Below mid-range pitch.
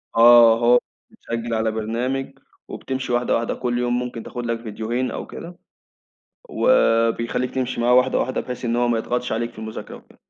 Yes: low, 120 Hz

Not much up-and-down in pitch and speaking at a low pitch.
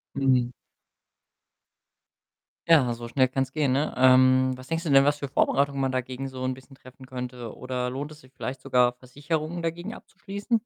Yes: narrow, 2.2 semitones; low, 130 Hz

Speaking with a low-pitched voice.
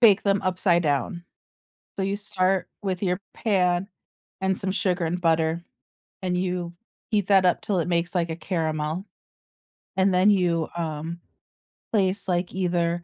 No: medium, 180 Hz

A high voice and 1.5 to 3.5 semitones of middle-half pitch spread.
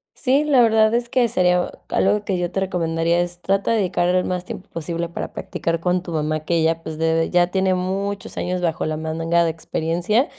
No: medium, 180 Hz; average, 3.0 semitones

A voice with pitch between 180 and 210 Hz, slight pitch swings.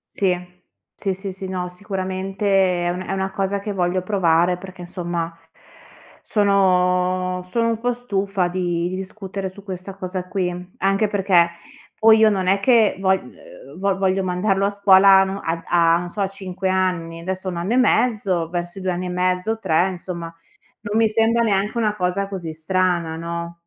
Yes: high, 190 Hz; narrow, 1.8 semitones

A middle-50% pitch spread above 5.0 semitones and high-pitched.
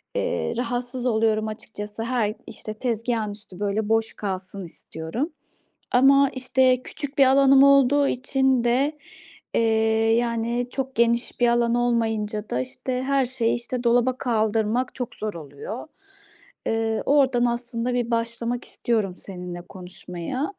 No: average, 3.0 semitones; high, 235 Hz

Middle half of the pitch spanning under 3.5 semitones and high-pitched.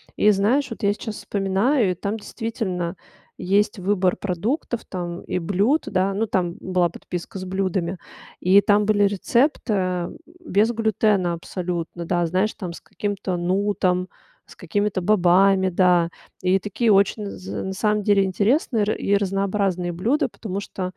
Yes: narrow, 2.4 semitones; high, 195 Hz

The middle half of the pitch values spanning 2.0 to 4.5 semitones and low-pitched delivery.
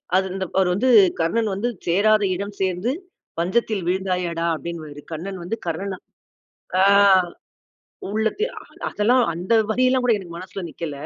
No: average, 4.1 semitones; high, 190 Hz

